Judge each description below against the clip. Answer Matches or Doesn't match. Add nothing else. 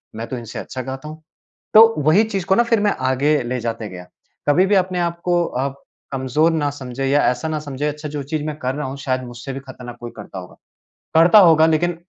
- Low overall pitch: Doesn't match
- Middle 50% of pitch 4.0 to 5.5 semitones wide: Matches